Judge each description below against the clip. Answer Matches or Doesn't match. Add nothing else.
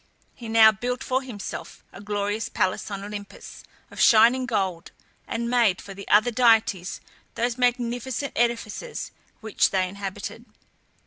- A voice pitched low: Doesn't match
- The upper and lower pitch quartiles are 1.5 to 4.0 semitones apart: Matches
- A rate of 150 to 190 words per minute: Doesn't match